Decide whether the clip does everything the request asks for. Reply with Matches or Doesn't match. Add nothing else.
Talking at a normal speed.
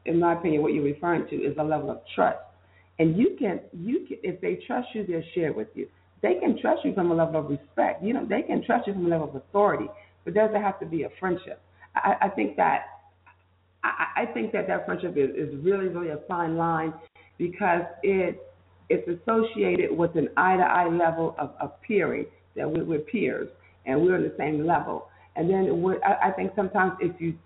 Doesn't match